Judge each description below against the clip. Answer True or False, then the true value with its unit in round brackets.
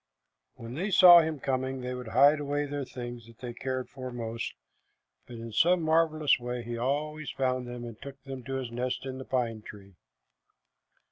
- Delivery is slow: False (190 wpm)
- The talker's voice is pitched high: False (130 Hz)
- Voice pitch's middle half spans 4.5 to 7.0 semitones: False (3.1 semitones)